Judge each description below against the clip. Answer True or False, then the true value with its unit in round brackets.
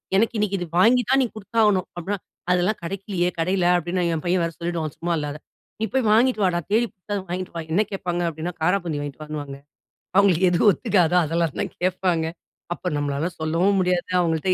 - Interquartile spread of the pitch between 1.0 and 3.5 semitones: True (3.1 semitones)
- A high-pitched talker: False (180 Hz)